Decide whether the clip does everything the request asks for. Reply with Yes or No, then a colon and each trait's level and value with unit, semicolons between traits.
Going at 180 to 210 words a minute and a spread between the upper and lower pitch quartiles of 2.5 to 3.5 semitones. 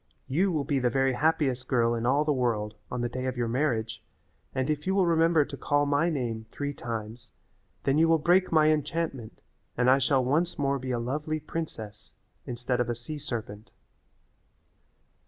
No: average, 190 wpm; average, 4.2 semitones